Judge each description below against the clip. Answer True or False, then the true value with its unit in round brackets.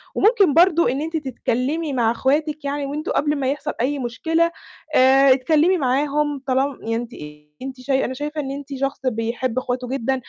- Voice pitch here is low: False (275 Hz)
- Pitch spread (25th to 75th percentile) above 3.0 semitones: False (2.7 semitones)